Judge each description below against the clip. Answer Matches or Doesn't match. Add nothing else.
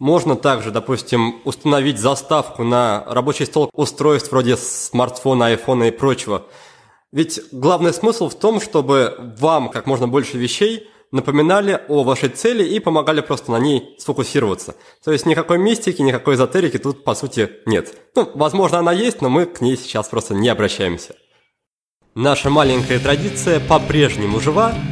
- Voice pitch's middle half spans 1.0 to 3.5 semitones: Doesn't match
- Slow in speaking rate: Doesn't match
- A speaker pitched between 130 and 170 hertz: Matches